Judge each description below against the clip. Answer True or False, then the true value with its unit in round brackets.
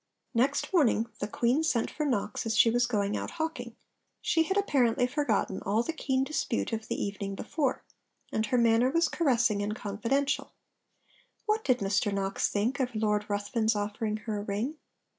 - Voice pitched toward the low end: False (230 Hz)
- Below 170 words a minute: False (175 wpm)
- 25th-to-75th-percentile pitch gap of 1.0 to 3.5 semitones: False (4.7 semitones)